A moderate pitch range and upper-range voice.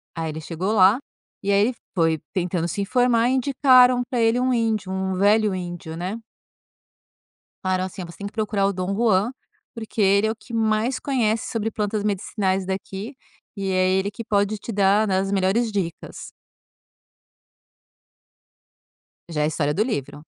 Yes: average, 3.2 semitones; high, 200 Hz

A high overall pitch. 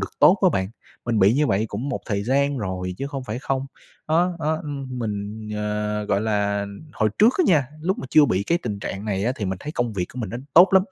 No: low, 115 Hz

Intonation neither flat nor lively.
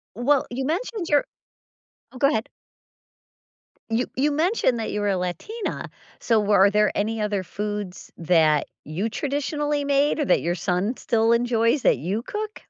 No: wide, 6.0 semitones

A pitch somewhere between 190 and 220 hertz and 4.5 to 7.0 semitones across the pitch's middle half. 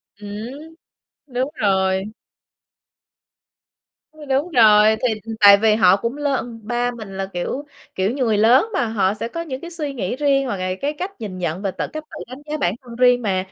No: high, 230 Hz; average, 5.2 semitones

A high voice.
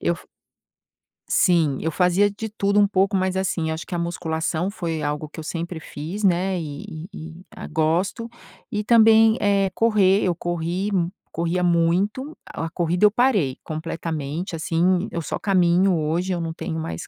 No: medium, 175 Hz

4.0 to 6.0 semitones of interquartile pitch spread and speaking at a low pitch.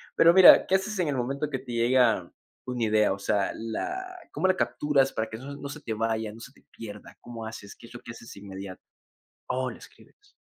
Yes: average, 4.9 semitones; low, 120 Hz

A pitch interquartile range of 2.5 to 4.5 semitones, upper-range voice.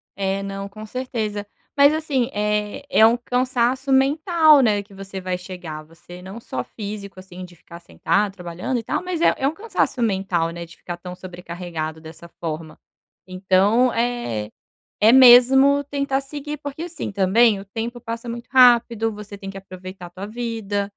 No: average, 5.2 semitones; high, 210 Hz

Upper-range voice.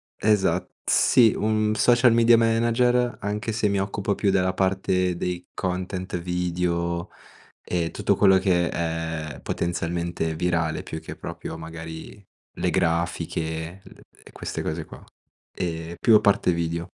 No: very low, 90 Hz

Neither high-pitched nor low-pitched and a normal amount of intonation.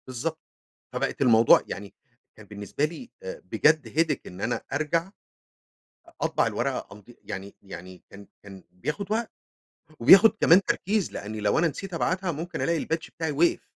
No: medium, 155 Hz; wide, 8.7 semitones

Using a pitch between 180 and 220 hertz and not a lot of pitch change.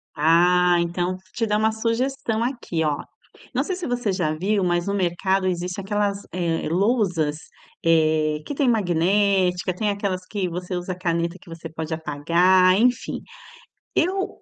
No: medium, 185 Hz; average, 3.6 semitones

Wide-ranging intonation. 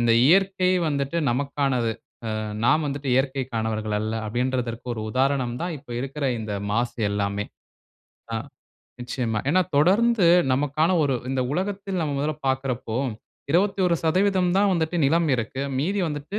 Yes: wide, 6.2 semitones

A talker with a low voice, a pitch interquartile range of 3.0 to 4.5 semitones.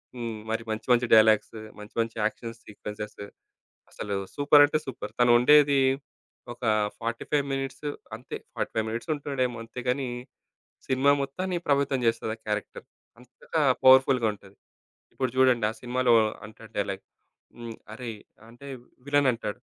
Yes: low, 120 Hz; average, 3.3 semitones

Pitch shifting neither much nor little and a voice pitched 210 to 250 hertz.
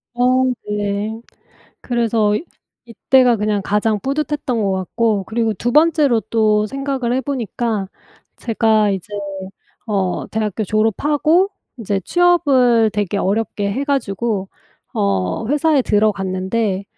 Yes: average, 4.0 semitones; high, 220 Hz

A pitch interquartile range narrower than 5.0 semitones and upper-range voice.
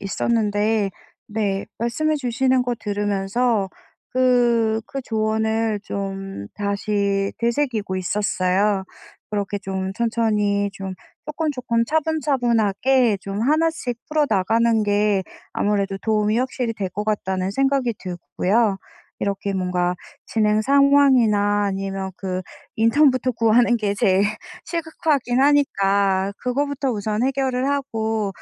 Yes: average, 4.0 semitones; high, 220 Hz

